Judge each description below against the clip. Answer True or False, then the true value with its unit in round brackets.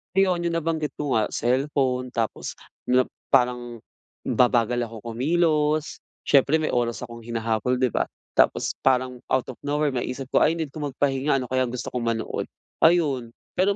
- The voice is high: False (130 Hz)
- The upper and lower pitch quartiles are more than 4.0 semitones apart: False (3.7 semitones)